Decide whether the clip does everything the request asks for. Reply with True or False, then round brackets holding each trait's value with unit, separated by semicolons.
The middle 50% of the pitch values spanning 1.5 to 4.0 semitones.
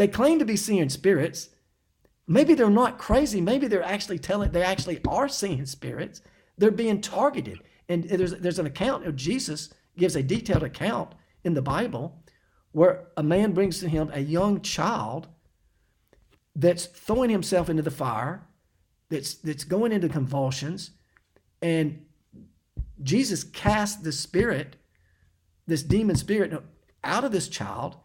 False (4.8 semitones)